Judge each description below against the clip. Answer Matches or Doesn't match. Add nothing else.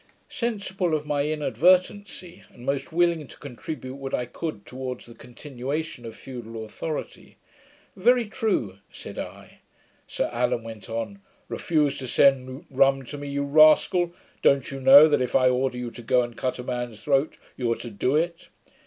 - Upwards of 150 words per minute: Matches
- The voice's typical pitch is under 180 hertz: Matches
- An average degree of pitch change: Matches